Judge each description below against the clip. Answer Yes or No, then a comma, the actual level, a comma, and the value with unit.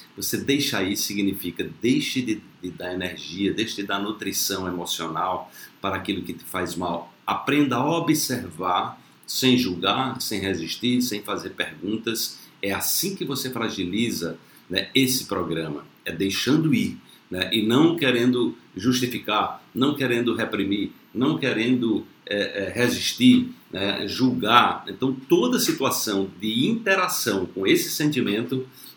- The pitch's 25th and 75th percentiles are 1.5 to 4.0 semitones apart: No, average, 5.2 semitones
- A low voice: Yes, low, 110 Hz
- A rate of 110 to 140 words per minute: Yes, average, 135 wpm